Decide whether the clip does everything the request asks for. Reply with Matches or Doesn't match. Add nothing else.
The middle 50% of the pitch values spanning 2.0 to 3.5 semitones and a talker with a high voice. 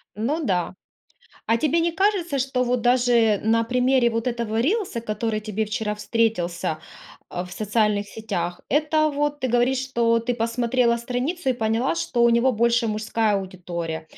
Matches